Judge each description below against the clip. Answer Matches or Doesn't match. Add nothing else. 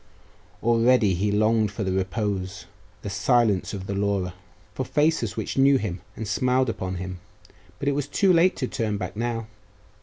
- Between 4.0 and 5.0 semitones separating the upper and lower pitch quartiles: Matches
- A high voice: Doesn't match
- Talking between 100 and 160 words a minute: Doesn't match